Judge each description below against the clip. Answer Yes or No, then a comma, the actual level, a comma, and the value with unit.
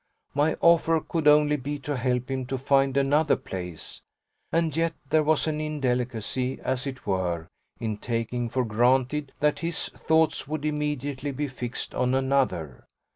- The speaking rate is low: No, average, 155 wpm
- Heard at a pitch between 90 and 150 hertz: Yes, low, 135 Hz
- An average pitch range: Yes, average, 3.2 semitones